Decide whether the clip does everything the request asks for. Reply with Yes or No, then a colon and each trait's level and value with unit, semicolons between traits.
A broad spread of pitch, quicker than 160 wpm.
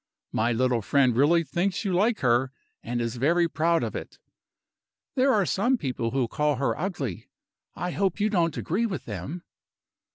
Yes: wide, 7.1 semitones; average, 170 wpm